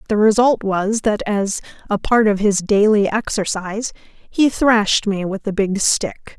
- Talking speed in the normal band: Yes, average, 170 wpm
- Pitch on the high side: Yes, high, 210 Hz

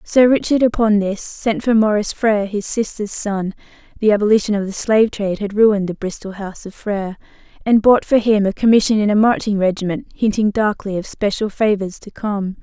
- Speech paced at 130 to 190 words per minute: Yes, average, 185 wpm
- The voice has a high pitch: Yes, high, 210 Hz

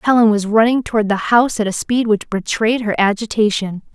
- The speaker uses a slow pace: No, average, 200 wpm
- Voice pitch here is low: No, high, 220 Hz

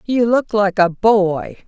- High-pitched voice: Yes, high, 205 Hz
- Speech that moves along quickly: No, average, 180 wpm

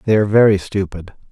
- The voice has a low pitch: Yes, low, 100 Hz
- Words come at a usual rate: Yes, average, 185 wpm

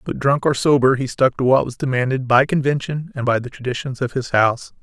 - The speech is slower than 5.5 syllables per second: No, 5.8 syllables/s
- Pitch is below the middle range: Yes, low, 130 Hz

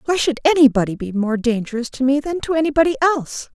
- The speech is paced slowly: No, average, 200 wpm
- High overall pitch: Yes, very high, 270 Hz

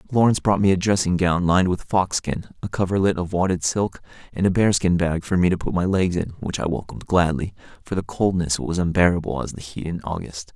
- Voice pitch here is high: No, very low, 90 Hz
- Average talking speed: No, fast, 225 wpm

